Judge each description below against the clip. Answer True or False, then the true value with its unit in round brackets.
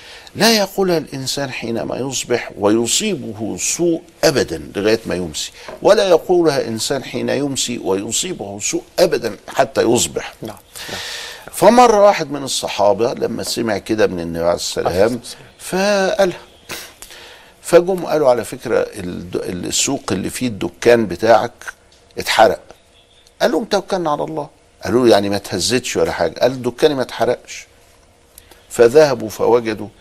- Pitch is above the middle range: False (125 Hz)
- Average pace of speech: True (120 wpm)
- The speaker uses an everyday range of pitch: False (8.2 semitones)